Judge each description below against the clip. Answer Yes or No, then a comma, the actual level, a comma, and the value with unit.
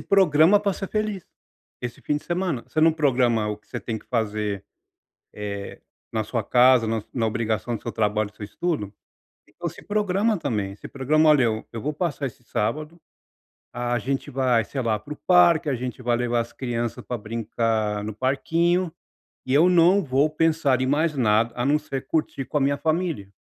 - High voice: No, low, 130 Hz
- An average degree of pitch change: No, wide, 5.9 semitones